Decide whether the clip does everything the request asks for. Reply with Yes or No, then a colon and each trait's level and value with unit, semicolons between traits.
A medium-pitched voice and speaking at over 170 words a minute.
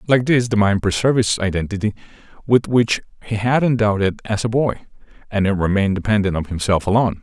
No: low, 105 Hz; average, 190 wpm